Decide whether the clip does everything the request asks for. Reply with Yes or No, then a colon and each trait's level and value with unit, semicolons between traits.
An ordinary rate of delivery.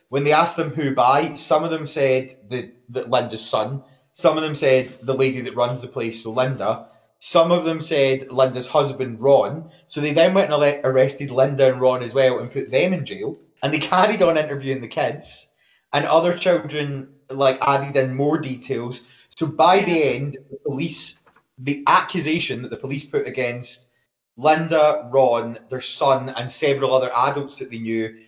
Yes: average, 185 wpm